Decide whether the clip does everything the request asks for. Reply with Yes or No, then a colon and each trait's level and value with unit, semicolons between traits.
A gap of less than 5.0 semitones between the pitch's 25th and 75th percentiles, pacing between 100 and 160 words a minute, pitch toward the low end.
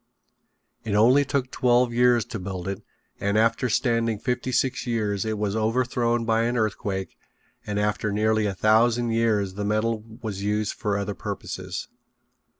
Yes: narrow, 2.5 semitones; average, 155 wpm; low, 110 Hz